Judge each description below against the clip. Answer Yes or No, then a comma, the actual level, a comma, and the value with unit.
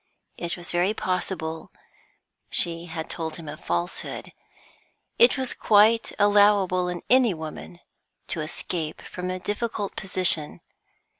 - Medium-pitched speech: Yes, medium, 180 Hz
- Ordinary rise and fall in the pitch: Yes, average, 4.0 semitones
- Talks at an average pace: No, slow, 125 wpm